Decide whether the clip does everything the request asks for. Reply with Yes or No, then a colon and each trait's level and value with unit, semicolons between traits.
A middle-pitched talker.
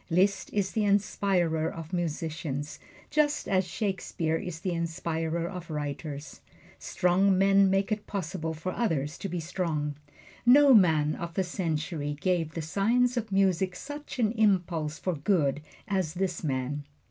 Yes: medium, 175 Hz